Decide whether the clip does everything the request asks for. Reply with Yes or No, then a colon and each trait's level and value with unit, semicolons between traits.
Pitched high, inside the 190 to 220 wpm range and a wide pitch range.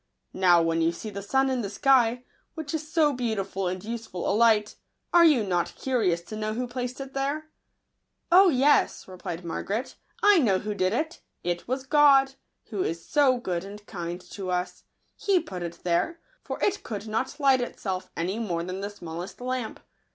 Yes: high, 220 Hz; average, 195 wpm; wide, 6.5 semitones